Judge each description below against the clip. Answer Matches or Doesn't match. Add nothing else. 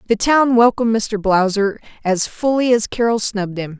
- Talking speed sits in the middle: Matches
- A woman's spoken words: Matches